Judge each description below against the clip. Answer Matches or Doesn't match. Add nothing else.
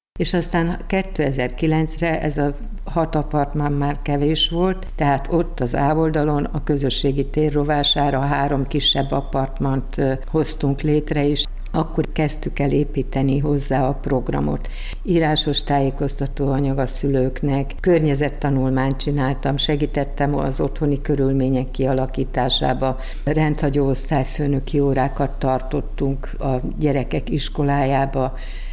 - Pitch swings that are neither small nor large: Doesn't match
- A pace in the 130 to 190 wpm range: Doesn't match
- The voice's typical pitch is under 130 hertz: Doesn't match